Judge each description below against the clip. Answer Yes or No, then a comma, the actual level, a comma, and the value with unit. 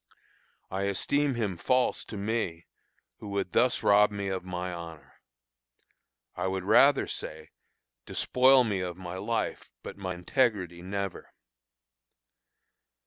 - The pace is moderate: No, slow, 125 wpm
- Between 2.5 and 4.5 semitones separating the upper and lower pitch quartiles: Yes, average, 3.8 semitones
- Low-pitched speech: Yes, low, 100 Hz